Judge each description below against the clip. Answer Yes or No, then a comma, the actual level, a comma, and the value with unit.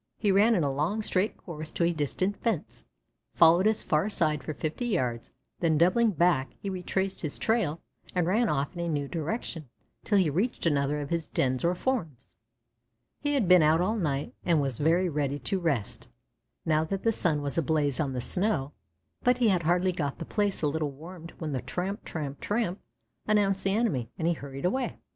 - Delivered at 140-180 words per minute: No, average, 200 wpm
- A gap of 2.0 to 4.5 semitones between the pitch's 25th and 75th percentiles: No, average, 4.9 semitones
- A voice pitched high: No, medium, 170 Hz